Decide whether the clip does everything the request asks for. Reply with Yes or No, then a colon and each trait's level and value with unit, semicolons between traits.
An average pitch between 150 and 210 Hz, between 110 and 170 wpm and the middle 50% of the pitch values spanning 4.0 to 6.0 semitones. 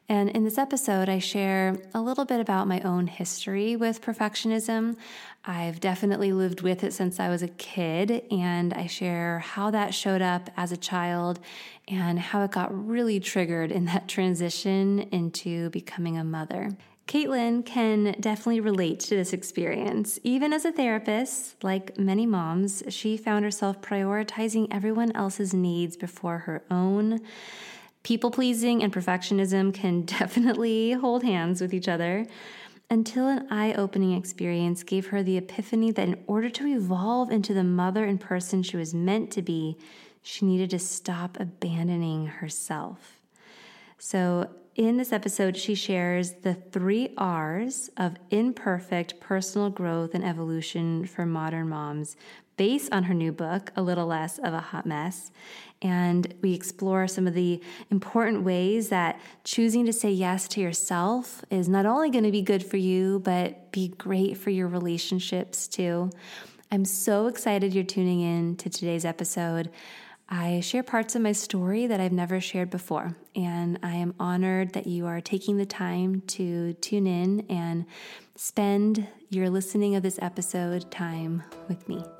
No: high, 190 Hz; average, 160 wpm; average, 3.1 semitones